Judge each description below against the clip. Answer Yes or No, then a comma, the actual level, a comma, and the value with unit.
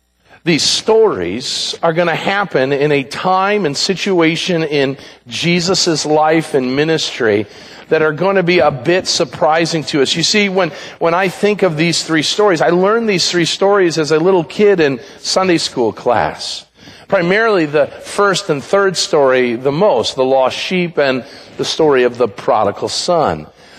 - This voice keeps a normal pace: Yes, average, 170 wpm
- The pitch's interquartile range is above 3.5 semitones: Yes, average, 4.1 semitones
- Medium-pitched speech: Yes, medium, 170 Hz